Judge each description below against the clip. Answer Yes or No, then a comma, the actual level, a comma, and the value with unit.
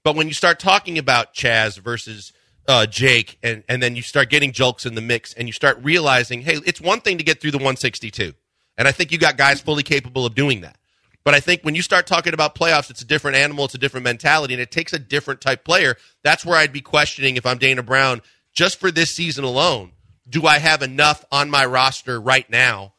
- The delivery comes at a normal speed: No, fast, 240 wpm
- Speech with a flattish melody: No, average, 3.8 semitones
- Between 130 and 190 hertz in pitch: Yes, low, 135 Hz